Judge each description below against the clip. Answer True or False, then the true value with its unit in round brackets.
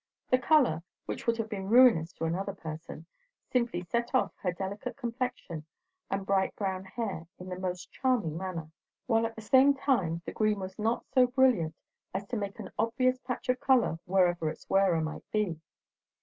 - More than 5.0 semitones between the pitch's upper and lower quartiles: True (5.4 semitones)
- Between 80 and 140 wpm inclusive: False (180 wpm)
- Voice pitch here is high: True (200 Hz)